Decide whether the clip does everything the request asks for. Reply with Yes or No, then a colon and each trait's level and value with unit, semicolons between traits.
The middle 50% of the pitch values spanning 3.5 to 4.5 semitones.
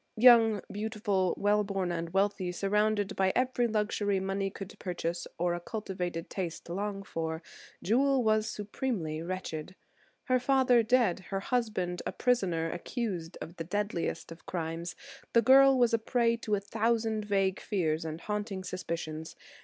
Yes: average, 4.1 semitones